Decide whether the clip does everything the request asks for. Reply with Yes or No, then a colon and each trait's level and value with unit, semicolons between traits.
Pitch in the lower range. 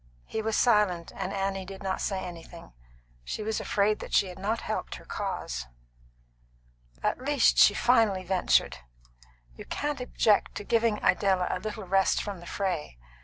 No: high, 195 Hz